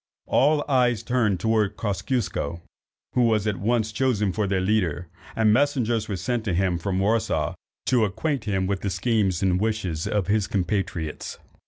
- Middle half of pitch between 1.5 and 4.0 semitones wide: Yes, average, 3.4 semitones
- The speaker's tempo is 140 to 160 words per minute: No, average, 170 wpm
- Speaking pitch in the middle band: No, low, 105 Hz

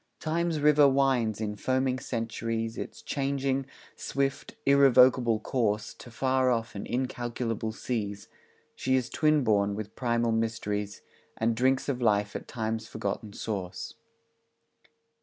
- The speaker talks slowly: Yes, slow, 125 wpm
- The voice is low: Yes, low, 120 Hz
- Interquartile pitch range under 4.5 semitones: Yes, average, 3.3 semitones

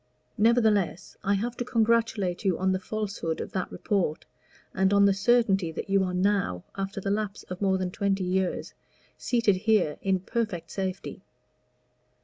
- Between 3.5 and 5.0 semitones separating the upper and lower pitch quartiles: No, narrow, 2.5 semitones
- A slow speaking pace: No, average, 160 wpm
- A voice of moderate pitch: No, high, 195 Hz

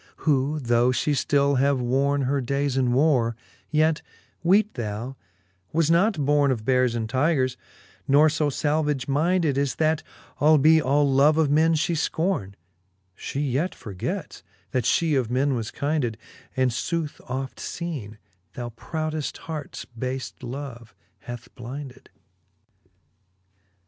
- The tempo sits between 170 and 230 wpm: No, slow, 135 wpm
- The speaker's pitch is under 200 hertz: Yes, medium, 140 Hz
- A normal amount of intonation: Yes, average, 3.5 semitones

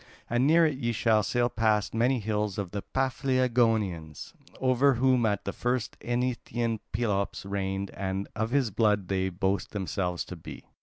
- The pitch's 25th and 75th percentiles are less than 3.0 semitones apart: No, average, 3.8 semitones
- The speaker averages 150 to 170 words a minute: Yes, average, 160 wpm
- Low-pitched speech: Yes, low, 110 Hz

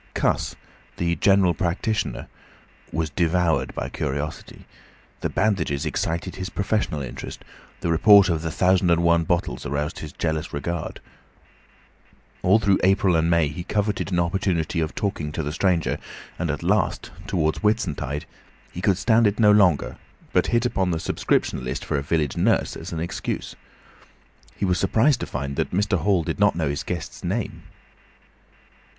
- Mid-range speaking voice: No, very low, 85 Hz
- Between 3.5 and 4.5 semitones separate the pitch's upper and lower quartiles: Yes, average, 3.9 semitones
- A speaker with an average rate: Yes, average, 160 wpm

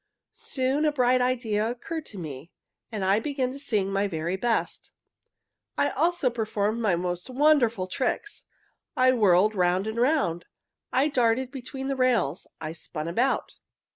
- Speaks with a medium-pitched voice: No, high, 230 Hz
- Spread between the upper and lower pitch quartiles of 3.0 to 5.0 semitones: No, wide, 5.6 semitones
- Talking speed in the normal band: Yes, average, 145 wpm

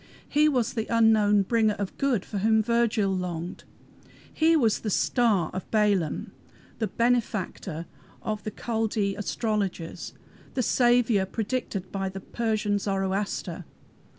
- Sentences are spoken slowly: Yes, slow, 125 wpm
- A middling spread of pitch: Yes, average, 3.2 semitones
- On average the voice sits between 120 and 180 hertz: No, high, 215 Hz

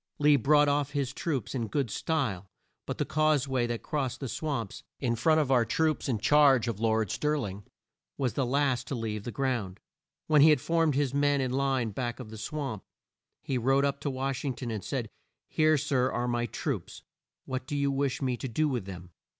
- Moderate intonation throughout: Yes, average, 3.3 semitones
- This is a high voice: No, low, 135 Hz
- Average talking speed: No, fast, 215 wpm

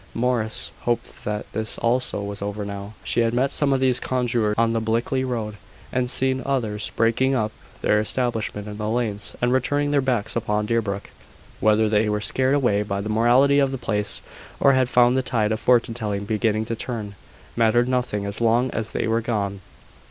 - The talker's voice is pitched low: Yes, low, 115 Hz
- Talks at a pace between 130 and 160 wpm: No, average, 195 wpm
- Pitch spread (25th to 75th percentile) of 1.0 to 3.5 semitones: Yes, average, 3.0 semitones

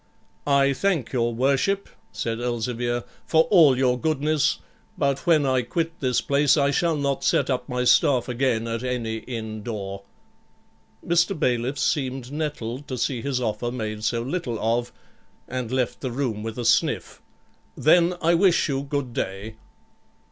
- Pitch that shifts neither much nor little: Yes, average, 3.5 semitones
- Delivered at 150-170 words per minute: Yes, average, 155 wpm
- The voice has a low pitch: Yes, low, 130 Hz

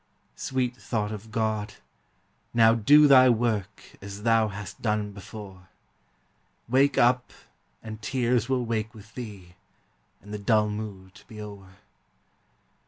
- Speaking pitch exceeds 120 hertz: No, low, 110 Hz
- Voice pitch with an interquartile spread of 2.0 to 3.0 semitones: Yes, narrow, 2.5 semitones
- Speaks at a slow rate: Yes, slow, 125 wpm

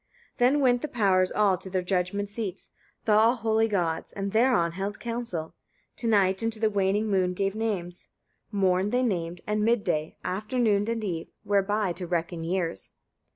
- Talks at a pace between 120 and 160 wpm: No, average, 180 wpm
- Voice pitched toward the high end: Yes, high, 200 Hz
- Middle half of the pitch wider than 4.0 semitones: No, average, 3.4 semitones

